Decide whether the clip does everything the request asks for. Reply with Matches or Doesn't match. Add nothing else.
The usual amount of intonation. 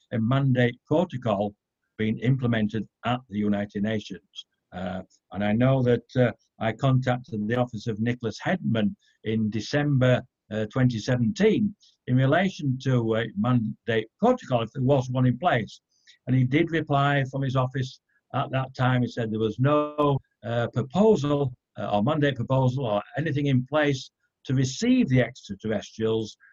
Matches